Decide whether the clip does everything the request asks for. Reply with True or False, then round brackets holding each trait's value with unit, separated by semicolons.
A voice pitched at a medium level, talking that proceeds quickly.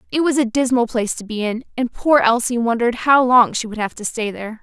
False (240 Hz; 260 wpm)